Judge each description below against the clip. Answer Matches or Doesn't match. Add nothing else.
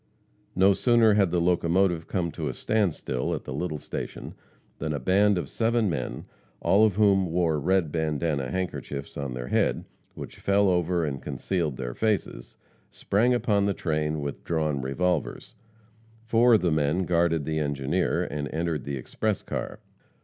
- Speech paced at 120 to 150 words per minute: Doesn't match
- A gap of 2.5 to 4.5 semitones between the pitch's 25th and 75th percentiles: Doesn't match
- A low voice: Matches